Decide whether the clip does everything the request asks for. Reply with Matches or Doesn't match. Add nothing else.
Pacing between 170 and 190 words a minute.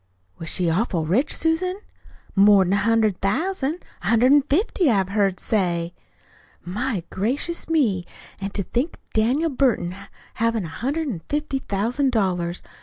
Doesn't match